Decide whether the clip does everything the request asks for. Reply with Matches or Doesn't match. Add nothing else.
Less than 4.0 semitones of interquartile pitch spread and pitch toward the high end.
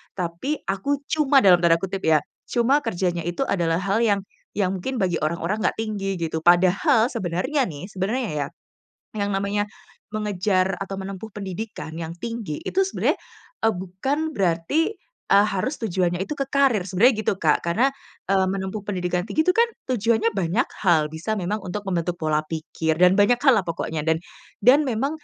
Doesn't match